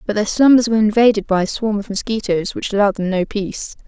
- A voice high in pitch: Yes, high, 210 Hz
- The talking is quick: Yes, fast, 230 wpm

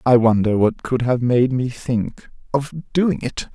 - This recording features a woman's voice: No, male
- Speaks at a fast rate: No, average, 185 wpm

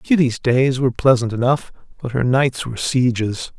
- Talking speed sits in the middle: Yes, average, 165 wpm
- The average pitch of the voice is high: No, low, 125 Hz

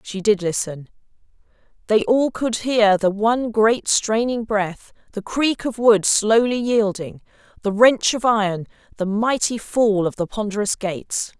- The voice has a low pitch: No, high, 215 Hz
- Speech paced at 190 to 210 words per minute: No, average, 155 wpm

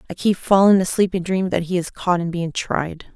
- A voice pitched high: No, medium, 180 Hz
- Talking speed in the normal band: No, fast, 245 wpm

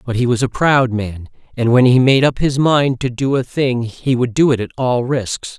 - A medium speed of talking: No, fast, 260 wpm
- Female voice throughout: No, male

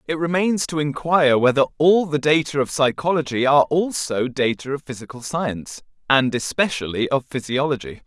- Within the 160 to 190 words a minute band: No, average, 150 wpm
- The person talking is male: Yes, male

